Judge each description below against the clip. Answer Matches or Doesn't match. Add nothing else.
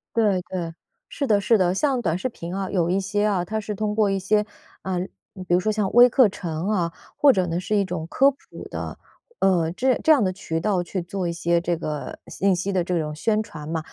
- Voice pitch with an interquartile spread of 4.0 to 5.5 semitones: Doesn't match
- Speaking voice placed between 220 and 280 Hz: Doesn't match